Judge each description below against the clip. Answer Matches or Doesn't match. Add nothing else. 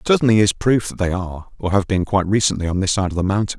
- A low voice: Matches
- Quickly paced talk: Matches